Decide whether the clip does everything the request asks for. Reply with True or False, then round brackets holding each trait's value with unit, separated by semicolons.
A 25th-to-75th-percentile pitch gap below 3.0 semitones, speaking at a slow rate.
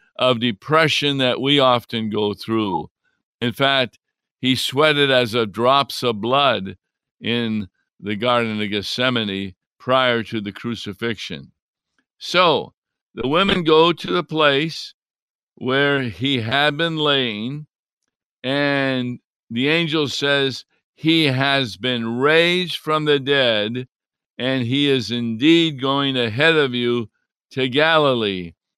False (3.7 semitones; 120 wpm)